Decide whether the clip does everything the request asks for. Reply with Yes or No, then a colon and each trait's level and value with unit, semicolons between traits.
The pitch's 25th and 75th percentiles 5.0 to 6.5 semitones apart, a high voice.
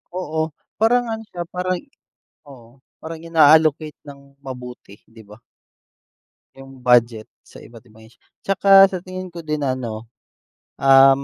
No: wide, 5.6 semitones; medium, 140 Hz